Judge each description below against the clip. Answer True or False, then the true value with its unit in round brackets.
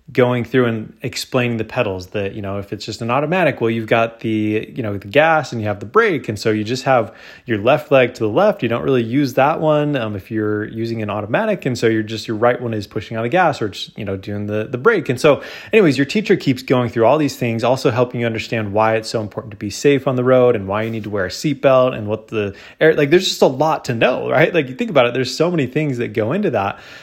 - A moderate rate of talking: False (300 wpm)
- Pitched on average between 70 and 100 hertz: False (115 Hz)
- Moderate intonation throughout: True (3.7 semitones)